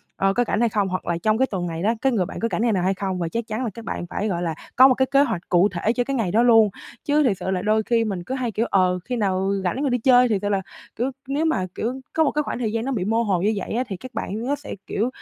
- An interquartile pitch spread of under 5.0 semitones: Yes, average, 4.6 semitones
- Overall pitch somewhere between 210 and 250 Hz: Yes, high, 220 Hz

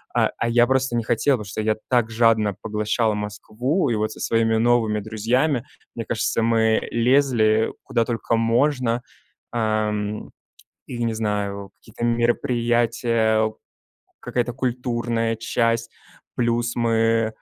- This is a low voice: Yes, low, 115 Hz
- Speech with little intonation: Yes, narrow, 1.5 semitones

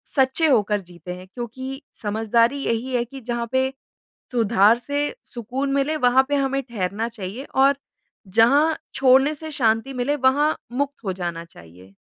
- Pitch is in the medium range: No, high, 245 Hz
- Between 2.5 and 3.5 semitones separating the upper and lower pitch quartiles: No, average, 4.1 semitones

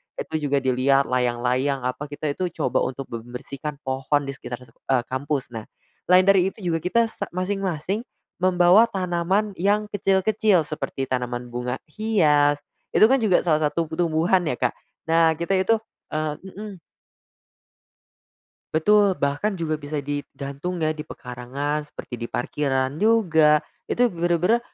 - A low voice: No, medium, 155 Hz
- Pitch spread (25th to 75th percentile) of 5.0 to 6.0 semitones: Yes, average, 5.3 semitones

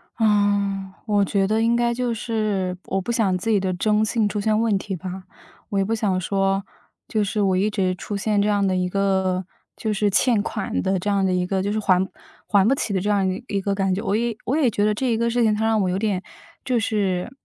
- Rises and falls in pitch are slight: Yes, narrow, 2.3 semitones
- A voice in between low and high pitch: No, high, 205 Hz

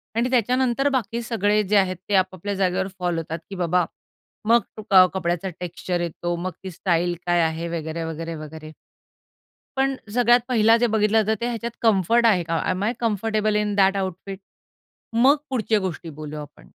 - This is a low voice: No, high, 195 Hz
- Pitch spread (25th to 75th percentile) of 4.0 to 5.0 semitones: Yes, average, 4.6 semitones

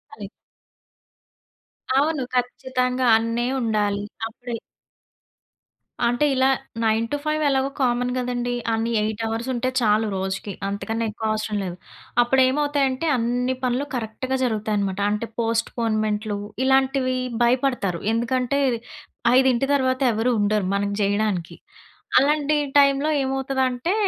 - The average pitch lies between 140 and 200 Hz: No, high, 240 Hz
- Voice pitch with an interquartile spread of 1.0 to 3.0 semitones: No, average, 3.4 semitones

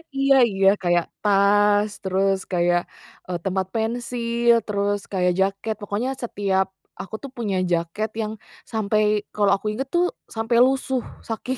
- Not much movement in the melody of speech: No, average, 3.3 semitones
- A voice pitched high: Yes, high, 205 Hz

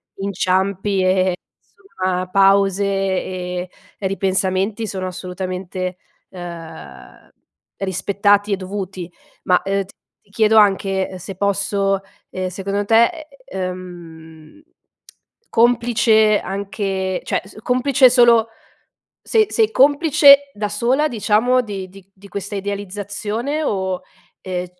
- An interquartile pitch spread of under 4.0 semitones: Yes, narrow, 2.6 semitones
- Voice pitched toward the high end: Yes, high, 195 Hz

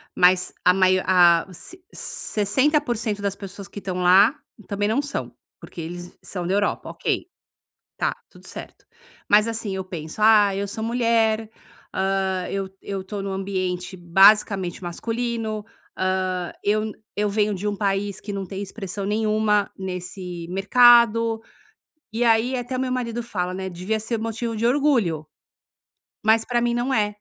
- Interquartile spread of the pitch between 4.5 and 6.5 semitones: No, average, 3.2 semitones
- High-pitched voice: Yes, high, 205 Hz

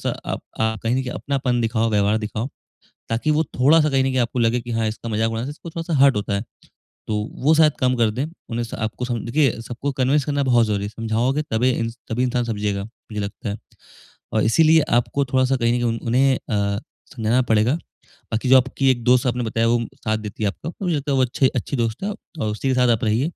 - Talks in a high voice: No, low, 120 Hz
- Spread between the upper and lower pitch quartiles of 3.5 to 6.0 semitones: No, average, 3.1 semitones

